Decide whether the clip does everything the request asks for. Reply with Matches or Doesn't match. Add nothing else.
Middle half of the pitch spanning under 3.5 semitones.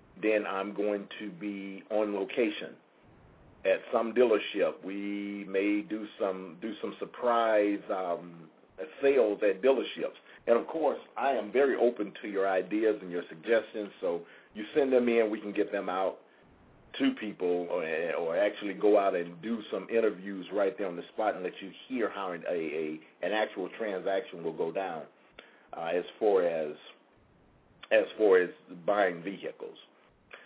Matches